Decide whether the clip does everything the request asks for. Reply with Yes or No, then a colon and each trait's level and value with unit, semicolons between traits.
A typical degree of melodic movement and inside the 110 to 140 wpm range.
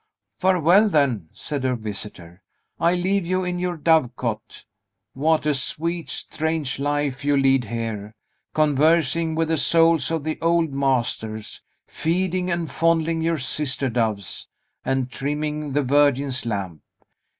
Yes: average, 4.5 semitones; slow, 135 wpm